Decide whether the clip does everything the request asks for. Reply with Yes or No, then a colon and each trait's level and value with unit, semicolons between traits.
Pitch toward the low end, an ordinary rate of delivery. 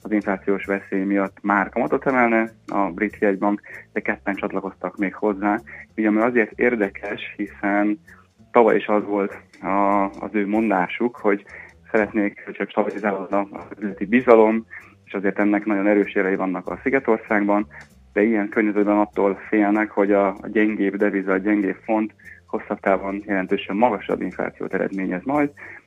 Yes: low, 105 Hz; average, 145 wpm